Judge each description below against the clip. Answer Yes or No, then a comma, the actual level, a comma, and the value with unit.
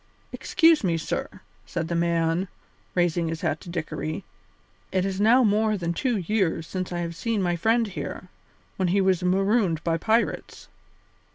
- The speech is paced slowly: No, average, 165 wpm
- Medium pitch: Yes, medium, 180 Hz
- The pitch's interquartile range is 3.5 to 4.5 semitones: Yes, average, 3.8 semitones